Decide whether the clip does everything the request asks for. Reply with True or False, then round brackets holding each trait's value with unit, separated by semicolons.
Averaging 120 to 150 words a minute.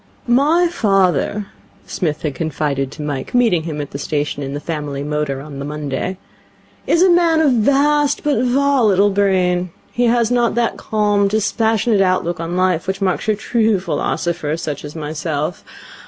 False (165 wpm)